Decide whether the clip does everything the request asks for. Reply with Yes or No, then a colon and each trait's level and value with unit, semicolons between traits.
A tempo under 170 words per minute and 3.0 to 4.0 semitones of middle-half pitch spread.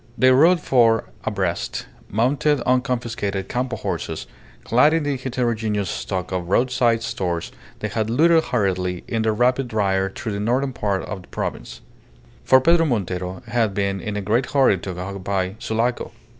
No: average, 160 wpm; average, 4.7 semitones